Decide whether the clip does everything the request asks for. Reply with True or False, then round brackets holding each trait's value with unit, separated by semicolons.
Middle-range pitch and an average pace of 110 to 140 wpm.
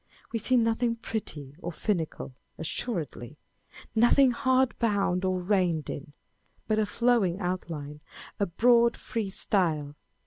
False (195 Hz; 135 wpm)